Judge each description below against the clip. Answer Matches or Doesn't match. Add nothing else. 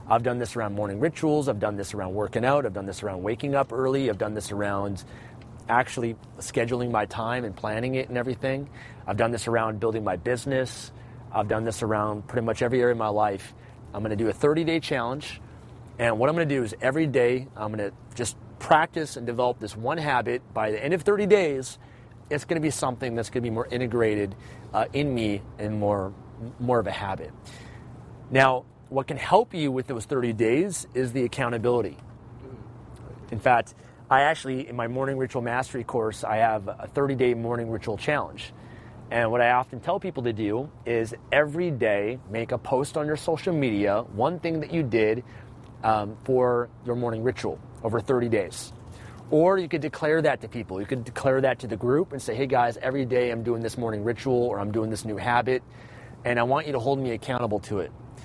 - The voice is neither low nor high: Doesn't match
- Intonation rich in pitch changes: Doesn't match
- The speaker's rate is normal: Doesn't match